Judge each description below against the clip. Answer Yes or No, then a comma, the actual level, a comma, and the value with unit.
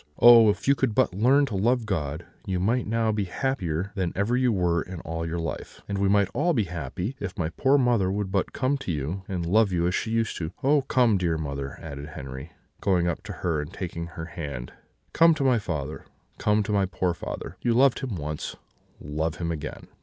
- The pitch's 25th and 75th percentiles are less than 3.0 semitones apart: No, wide, 5.6 semitones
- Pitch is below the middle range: Yes, very low, 95 Hz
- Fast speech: Yes, fast, 225 wpm